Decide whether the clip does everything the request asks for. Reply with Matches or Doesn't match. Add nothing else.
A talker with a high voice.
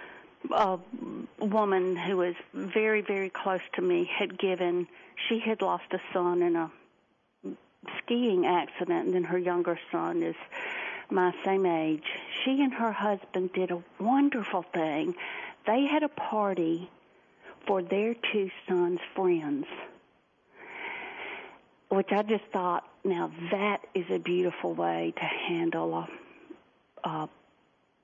Matches